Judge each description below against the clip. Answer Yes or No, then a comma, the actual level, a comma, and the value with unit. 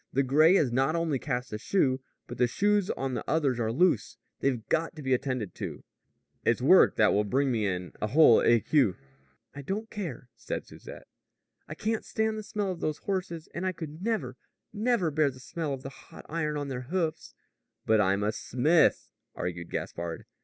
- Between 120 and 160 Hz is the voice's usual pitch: Yes, medium, 140 Hz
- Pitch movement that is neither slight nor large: No, wide, 5.7 semitones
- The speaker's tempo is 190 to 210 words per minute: Yes, average, 195 wpm